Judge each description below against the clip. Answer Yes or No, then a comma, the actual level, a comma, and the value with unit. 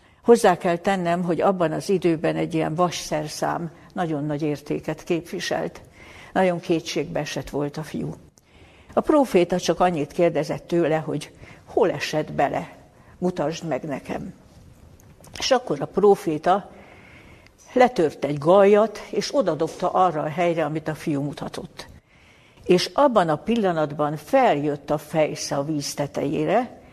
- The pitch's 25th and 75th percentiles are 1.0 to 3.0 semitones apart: No, average, 3.6 semitones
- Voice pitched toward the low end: No, medium, 165 Hz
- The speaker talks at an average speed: Yes, average, 130 wpm